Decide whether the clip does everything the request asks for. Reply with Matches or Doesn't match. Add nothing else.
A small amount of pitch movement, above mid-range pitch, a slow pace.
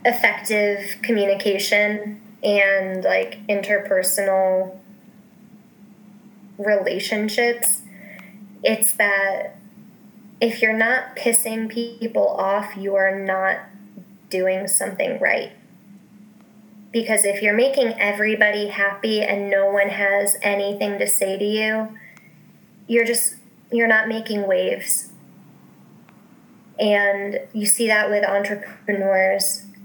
Matches